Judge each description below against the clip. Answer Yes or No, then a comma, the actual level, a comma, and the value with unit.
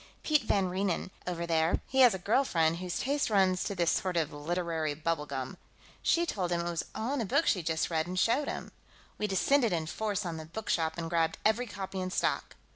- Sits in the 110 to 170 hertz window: No, medium, 180 Hz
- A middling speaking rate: No, fast, 225 wpm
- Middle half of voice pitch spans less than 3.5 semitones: No, average, 4.3 semitones